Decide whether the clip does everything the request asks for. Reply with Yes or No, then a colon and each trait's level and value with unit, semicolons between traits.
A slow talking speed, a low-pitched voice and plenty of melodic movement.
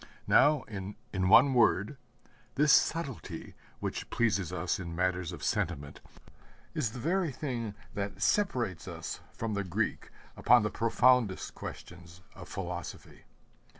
Yes: slow, 125 wpm; low, 115 Hz; wide, 5.9 semitones